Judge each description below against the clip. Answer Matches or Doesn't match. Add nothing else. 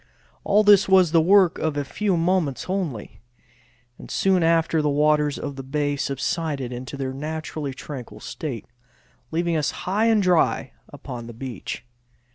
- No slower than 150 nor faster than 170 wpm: Matches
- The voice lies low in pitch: Doesn't match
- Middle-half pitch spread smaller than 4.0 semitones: Doesn't match